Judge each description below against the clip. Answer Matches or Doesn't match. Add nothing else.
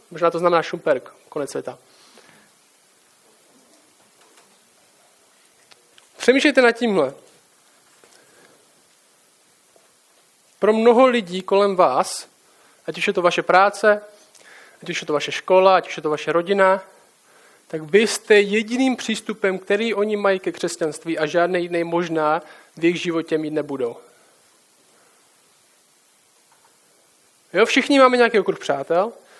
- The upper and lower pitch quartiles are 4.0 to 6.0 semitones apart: Matches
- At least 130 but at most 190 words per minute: Doesn't match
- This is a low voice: Doesn't match